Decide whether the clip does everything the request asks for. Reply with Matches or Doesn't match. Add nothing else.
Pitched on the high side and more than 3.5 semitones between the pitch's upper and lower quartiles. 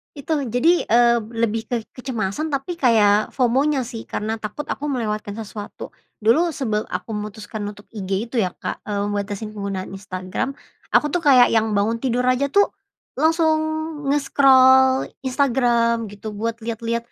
Matches